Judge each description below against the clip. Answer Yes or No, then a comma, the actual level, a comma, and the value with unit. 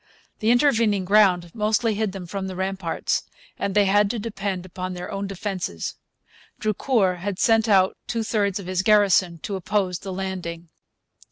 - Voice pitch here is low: No, high, 195 Hz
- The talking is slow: No, average, 165 wpm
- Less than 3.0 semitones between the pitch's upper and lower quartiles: Yes, narrow, 2.4 semitones